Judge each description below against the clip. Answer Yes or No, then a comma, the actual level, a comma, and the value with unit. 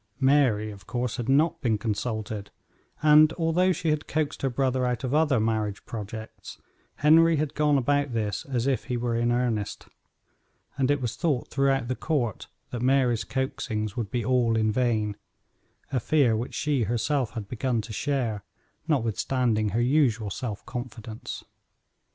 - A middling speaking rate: Yes, average, 160 wpm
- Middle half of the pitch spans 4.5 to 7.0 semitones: No, average, 3.9 semitones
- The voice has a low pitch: Yes, low, 125 Hz